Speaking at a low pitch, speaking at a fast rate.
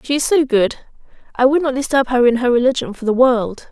No: very high, 255 Hz; fast, 225 wpm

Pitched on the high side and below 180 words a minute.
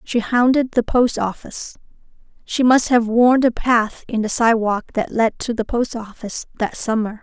No: high, 230 Hz; average, 185 wpm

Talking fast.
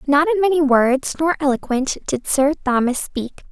No: average, 170 wpm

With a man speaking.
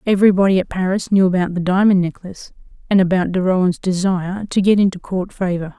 No: female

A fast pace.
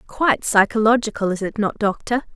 No: average, 155 wpm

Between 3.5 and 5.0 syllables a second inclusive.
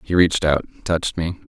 No: 6.1 syllables/s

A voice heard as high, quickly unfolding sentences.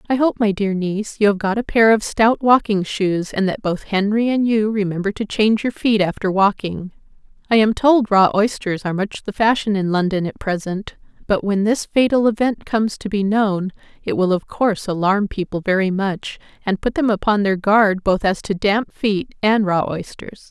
Yes: high, 205 Hz; fast, 210 wpm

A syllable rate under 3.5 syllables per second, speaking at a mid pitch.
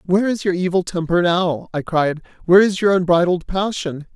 No: 5.4 syllables/s; medium, 180 Hz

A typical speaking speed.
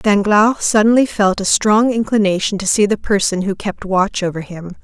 Yes: average, 185 wpm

